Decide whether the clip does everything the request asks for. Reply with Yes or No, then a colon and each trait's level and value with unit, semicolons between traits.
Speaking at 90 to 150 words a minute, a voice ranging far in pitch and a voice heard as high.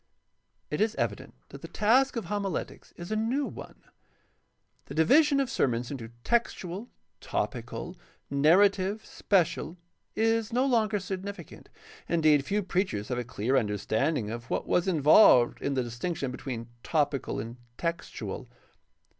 No: average, 140 wpm; wide, 8.5 semitones; medium, 170 Hz